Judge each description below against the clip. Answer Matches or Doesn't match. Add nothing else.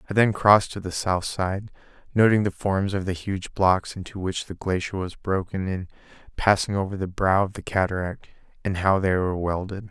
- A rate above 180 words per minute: Matches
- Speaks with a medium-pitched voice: Doesn't match